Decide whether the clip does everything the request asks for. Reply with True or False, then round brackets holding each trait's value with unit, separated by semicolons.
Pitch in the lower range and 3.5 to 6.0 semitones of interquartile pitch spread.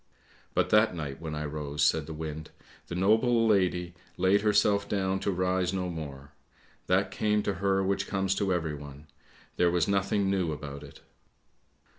True (90 Hz; 4.2 semitones)